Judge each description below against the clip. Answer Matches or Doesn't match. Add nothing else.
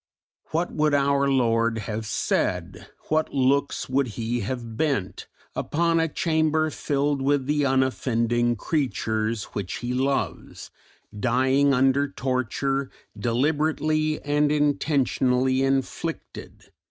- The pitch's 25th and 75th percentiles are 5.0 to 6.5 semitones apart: Doesn't match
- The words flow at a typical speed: Doesn't match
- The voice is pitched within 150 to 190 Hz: Doesn't match